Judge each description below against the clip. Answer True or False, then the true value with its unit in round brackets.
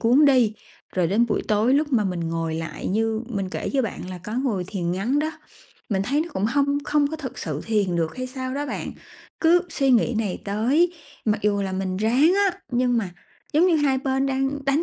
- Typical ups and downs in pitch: False (6.1 semitones)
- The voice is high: True (235 Hz)